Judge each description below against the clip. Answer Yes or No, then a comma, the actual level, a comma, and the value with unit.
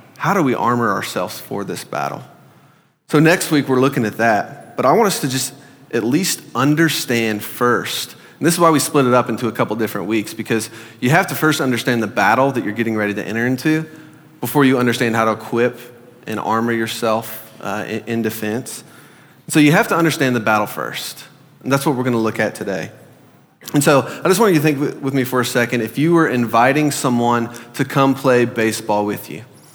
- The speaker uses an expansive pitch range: No, average, 4.0 semitones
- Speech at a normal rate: No, fast, 215 wpm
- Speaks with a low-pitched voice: Yes, low, 120 Hz